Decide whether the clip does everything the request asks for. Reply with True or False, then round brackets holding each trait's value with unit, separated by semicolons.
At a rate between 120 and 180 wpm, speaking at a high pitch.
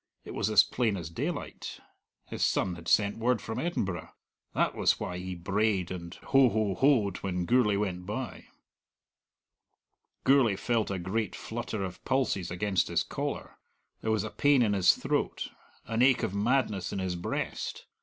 False (165 wpm; 105 Hz)